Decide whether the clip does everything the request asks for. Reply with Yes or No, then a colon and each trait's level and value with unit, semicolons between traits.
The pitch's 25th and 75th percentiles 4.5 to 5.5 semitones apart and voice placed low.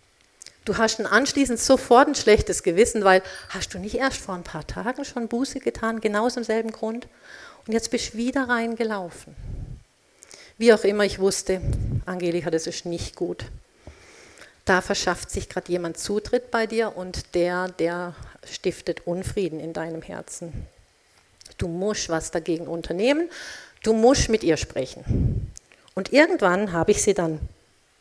No: average, 5.0 semitones; high, 205 Hz